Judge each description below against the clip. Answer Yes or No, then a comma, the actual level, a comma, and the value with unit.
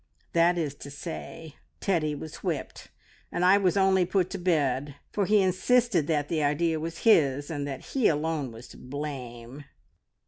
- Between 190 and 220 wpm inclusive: No, average, 170 wpm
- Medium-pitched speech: Yes, medium, 160 Hz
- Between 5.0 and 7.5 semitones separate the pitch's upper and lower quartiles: No, average, 4.3 semitones